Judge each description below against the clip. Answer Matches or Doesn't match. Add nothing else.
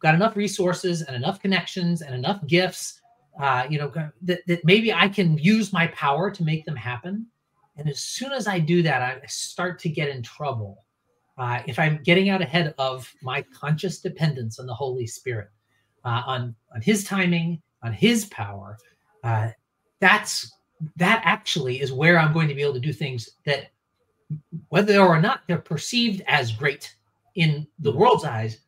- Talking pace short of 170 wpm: Doesn't match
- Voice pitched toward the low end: Doesn't match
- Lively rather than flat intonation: Matches